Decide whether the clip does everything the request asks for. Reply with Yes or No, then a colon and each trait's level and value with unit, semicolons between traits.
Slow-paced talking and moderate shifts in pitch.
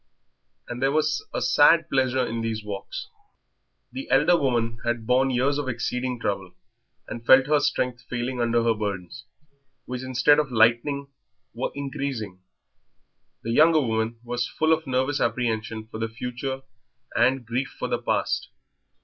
No: average, 150 wpm; average, 3.0 semitones